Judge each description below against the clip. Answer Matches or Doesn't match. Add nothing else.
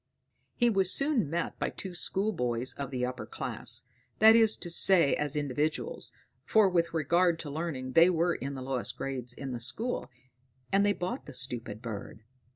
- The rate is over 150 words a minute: Matches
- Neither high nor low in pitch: Matches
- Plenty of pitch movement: Matches